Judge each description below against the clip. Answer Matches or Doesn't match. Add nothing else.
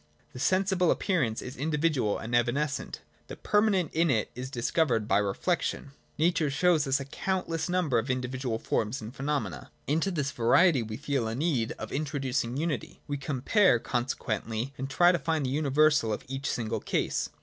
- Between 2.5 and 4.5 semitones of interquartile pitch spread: Doesn't match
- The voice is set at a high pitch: Doesn't match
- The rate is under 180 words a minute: Matches